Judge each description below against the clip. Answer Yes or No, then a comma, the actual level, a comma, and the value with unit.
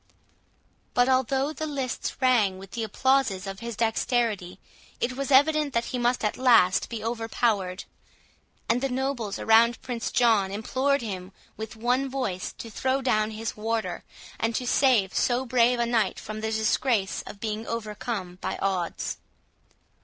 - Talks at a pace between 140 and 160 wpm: Yes, average, 155 wpm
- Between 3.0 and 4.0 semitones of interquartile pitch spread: Yes, average, 3.3 semitones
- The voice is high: Yes, high, 230 Hz